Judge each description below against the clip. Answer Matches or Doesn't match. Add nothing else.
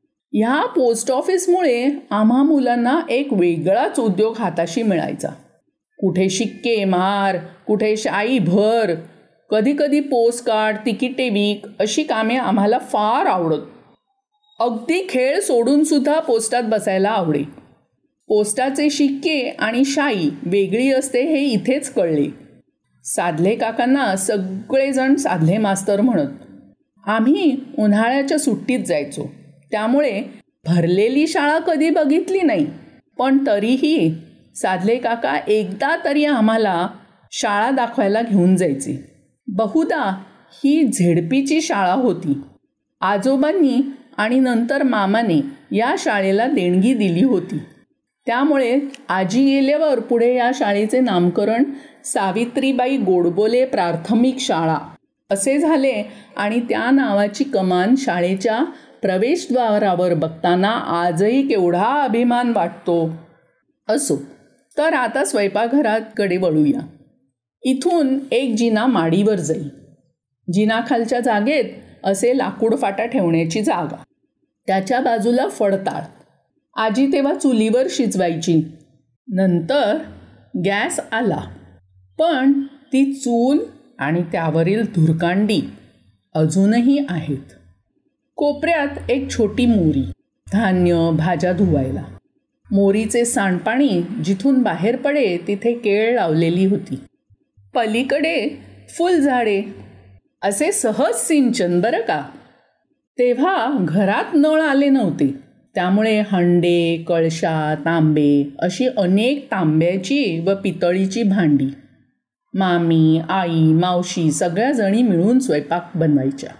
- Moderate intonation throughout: Doesn't match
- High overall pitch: Matches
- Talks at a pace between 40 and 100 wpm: Matches